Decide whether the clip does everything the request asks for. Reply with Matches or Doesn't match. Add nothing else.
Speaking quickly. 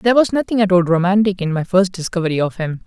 Matches